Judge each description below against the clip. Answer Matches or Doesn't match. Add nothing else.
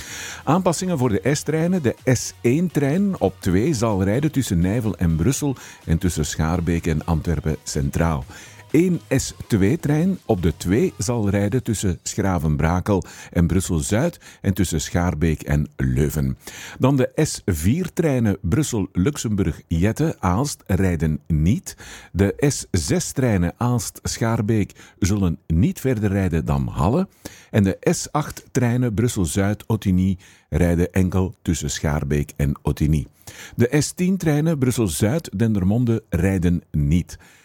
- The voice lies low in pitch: Matches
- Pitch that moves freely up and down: Matches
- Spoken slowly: Matches